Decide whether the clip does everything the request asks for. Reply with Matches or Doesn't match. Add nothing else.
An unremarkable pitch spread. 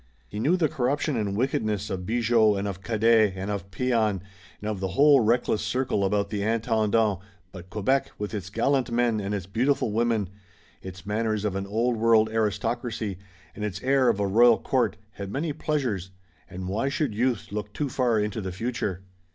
Matches